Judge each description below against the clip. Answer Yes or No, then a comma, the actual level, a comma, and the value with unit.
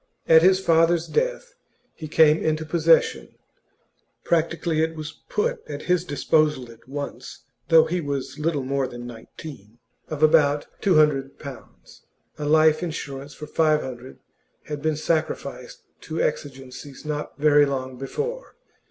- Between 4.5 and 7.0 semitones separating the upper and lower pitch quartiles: No, average, 2.9 semitones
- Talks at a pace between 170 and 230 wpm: No, average, 140 wpm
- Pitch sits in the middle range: Yes, medium, 155 Hz